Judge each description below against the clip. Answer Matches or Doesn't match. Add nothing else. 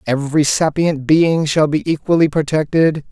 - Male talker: Matches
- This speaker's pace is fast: Doesn't match